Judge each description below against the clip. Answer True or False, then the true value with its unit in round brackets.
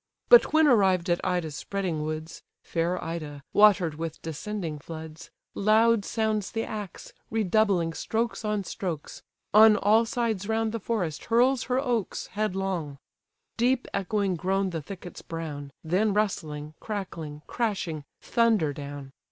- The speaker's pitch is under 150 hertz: False (195 Hz)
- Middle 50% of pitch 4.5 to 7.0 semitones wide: True (5.2 semitones)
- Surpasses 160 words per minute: False (135 wpm)